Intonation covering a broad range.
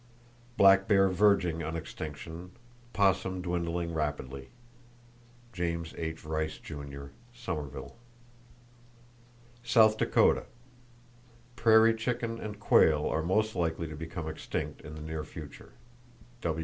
Yes: wide, 5.7 semitones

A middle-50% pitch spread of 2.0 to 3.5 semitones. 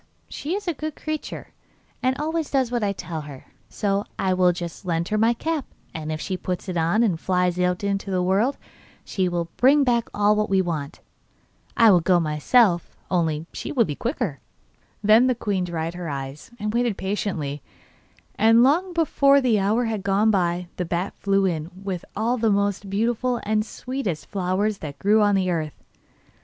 No: average, 5.1 semitones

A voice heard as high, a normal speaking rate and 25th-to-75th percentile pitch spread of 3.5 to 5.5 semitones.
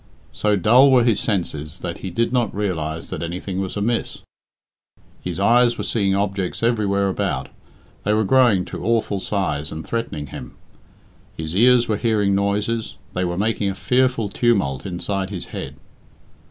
No: low, 100 Hz; average, 160 wpm; average, 4.1 semitones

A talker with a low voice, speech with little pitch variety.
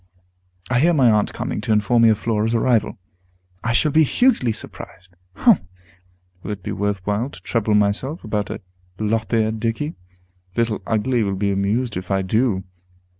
No: low, 110 Hz; average, 3.0 semitones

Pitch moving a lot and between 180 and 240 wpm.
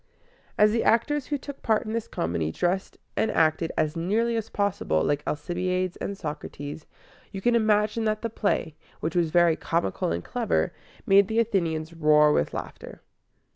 No: wide, 5.8 semitones; average, 170 wpm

